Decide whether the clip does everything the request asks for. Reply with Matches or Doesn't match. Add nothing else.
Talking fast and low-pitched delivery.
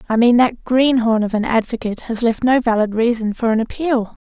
Doesn't match